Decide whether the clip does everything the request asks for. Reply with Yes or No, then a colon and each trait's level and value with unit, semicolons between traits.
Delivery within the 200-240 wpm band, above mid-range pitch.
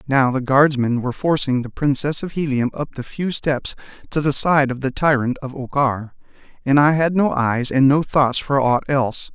No: fast, 205 wpm; low, 135 Hz